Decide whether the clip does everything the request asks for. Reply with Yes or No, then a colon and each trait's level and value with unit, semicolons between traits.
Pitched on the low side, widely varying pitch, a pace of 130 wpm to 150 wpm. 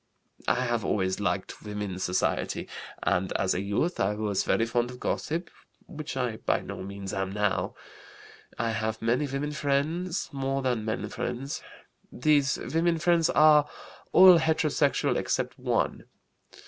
Yes: low, 125 Hz; wide, 6.5 semitones; average, 145 wpm